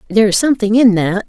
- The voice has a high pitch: Yes, high, 210 Hz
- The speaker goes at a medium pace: No, fast, 235 wpm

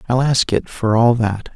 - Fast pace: Yes, fast, 230 wpm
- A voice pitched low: Yes, low, 120 Hz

